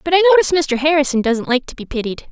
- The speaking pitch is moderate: No, very high, 295 Hz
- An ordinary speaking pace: No, fast, 260 wpm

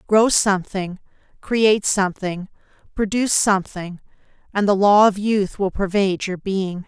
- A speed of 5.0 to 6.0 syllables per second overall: No, 4.8 syllables/s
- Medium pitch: No, high, 195 Hz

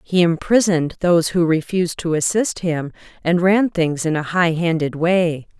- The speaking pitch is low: No, medium, 170 Hz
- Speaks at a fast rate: No, average, 170 wpm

